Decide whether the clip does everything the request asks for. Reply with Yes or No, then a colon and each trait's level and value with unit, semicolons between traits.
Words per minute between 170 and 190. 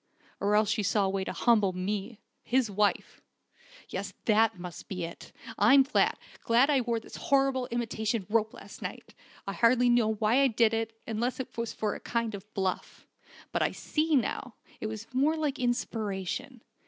Yes: average, 180 wpm